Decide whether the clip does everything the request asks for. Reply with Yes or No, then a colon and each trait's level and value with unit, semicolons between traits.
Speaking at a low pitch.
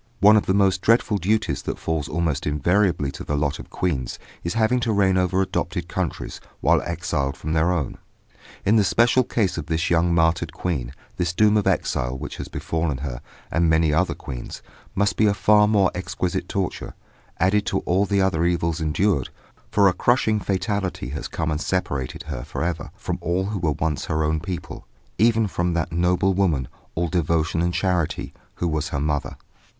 Yes: very low, 85 Hz